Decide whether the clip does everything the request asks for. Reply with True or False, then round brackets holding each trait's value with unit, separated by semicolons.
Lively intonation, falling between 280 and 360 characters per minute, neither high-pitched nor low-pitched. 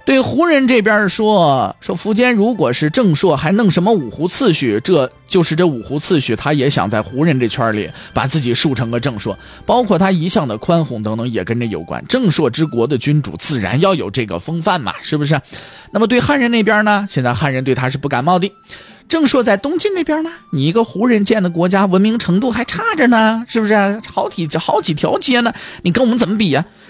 True (7.9 semitones; 320 characters per minute; 180 Hz)